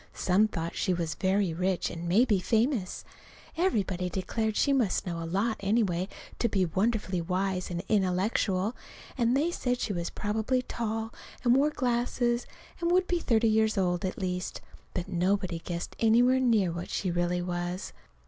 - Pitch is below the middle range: No, high, 200 Hz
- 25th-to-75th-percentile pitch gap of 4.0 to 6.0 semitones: Yes, average, 4.6 semitones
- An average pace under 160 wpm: No, average, 165 wpm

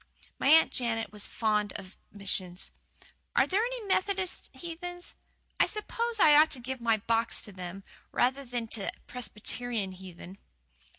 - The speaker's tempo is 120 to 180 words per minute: Yes, average, 145 wpm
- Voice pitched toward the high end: Yes, high, 235 Hz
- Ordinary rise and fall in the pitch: No, wide, 8.1 semitones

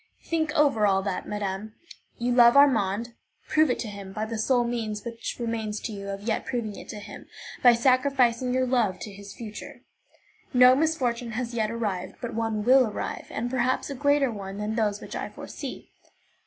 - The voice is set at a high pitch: Yes, high, 230 Hz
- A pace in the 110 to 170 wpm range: No, average, 190 wpm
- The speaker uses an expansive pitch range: No, average, 3.3 semitones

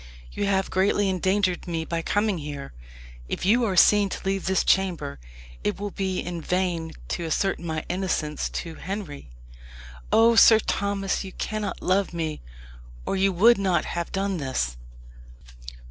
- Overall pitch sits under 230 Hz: Yes, medium, 185 Hz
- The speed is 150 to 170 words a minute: Yes, average, 155 wpm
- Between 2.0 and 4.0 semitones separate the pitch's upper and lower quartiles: Yes, average, 3.1 semitones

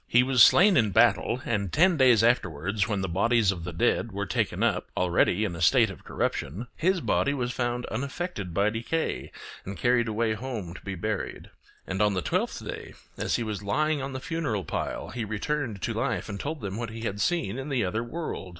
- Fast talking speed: Yes, fast, 215 wpm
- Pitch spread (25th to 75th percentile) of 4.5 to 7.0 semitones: Yes, average, 4.9 semitones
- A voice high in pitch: No, low, 115 Hz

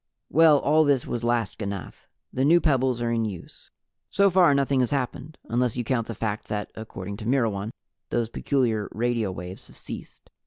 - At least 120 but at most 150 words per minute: No, average, 185 wpm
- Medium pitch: No, low, 120 Hz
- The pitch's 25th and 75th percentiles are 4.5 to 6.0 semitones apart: No, average, 4.1 semitones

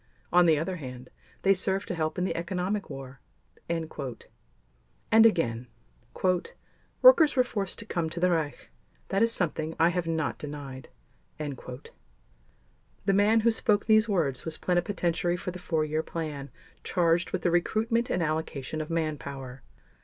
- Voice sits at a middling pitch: Yes, medium, 170 Hz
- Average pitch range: Yes, average, 4.5 semitones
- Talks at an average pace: Yes, average, 150 wpm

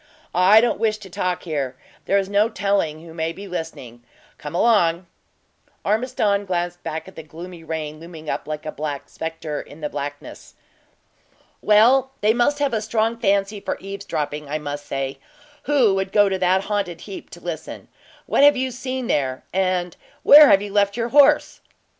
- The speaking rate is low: No, average, 175 wpm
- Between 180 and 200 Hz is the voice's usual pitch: Yes, high, 190 Hz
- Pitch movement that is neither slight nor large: Yes, average, 5.0 semitones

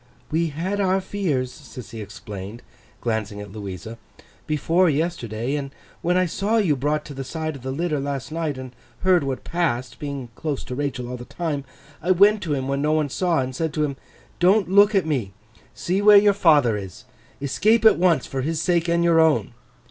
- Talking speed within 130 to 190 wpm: No, average, 200 wpm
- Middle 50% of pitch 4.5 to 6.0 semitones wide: Yes, wide, 5.4 semitones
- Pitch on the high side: No, medium, 150 Hz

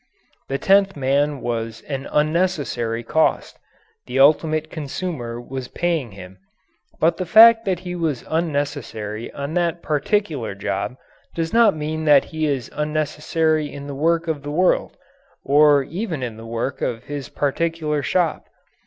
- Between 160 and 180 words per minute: No, average, 145 wpm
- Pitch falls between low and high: Yes, medium, 150 Hz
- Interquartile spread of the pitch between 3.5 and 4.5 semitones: Yes, average, 3.9 semitones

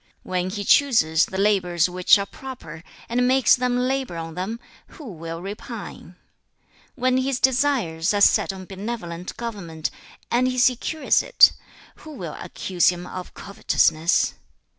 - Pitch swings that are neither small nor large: No, wide, 6.1 semitones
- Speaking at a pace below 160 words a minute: Yes, average, 140 wpm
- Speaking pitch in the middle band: No, high, 200 Hz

